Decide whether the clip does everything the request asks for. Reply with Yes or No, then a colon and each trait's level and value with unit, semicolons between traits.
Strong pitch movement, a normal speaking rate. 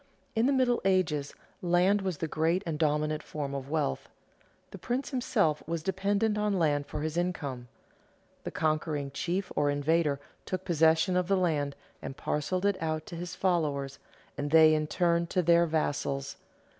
No: average, 3.7 semitones; average, 170 wpm